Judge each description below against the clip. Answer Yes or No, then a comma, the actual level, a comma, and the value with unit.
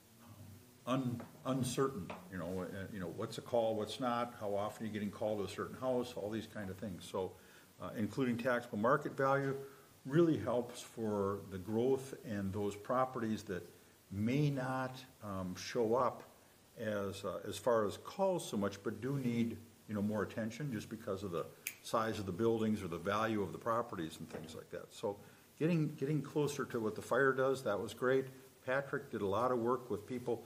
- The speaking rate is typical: Yes, average, 195 wpm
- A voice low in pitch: Yes, low, 115 Hz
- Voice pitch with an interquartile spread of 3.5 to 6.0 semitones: Yes, average, 4.0 semitones